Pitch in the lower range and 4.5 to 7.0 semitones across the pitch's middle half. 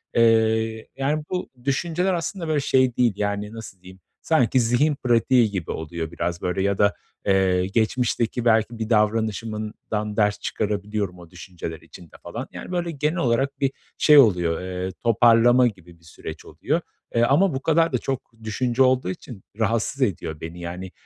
Yes: low, 110 Hz; average, 5.3 semitones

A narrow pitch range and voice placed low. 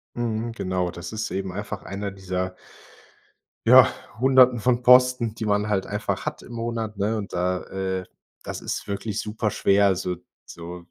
No: average, 3.4 semitones; low, 100 Hz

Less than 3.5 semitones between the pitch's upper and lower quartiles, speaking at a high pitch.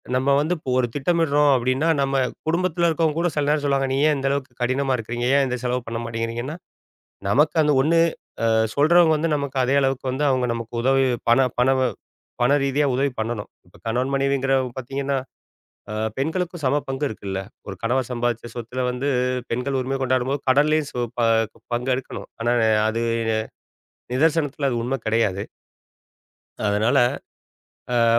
No: average, 3.0 semitones; low, 135 Hz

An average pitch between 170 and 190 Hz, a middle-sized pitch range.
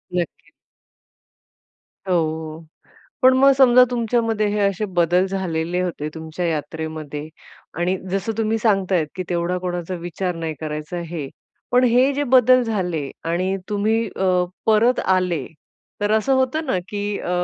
Yes: medium, 185 Hz; average, 5.0 semitones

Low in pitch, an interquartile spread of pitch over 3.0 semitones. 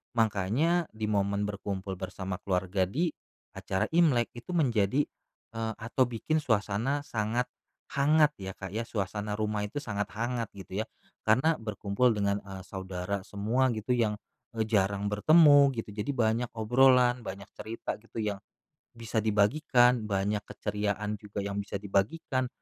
Yes: low, 110 Hz; average, 3.5 semitones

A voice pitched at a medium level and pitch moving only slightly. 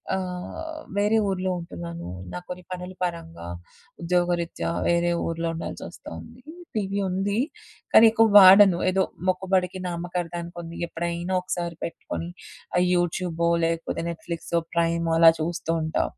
Yes: medium, 175 Hz; narrow, 1.8 semitones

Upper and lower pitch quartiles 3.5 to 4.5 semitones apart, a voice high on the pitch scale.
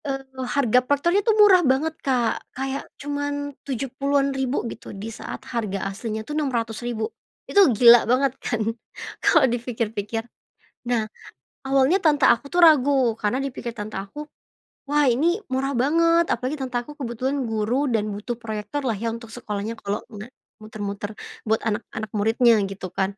Yes: average, 4.2 semitones; high, 245 Hz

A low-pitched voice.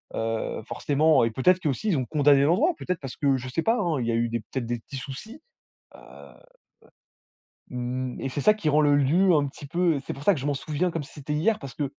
No: medium, 145 Hz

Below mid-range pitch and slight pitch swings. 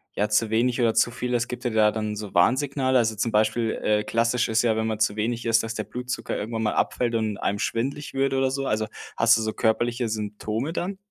Yes: low, 115 Hz; narrow, 2.3 semitones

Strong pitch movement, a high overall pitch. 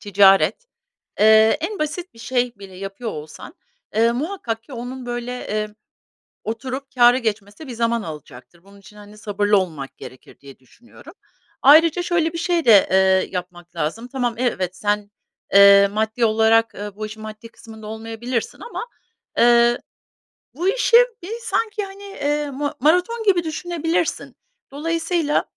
Yes: wide, 6.3 semitones; high, 230 Hz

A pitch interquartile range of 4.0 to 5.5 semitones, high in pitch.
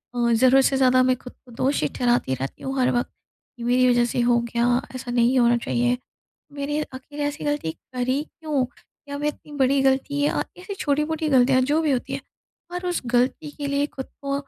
No: average, 2.9 semitones; very high, 265 Hz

